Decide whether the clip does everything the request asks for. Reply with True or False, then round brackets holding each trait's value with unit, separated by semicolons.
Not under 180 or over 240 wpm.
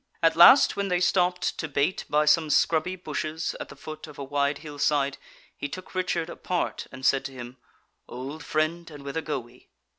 True (200 wpm)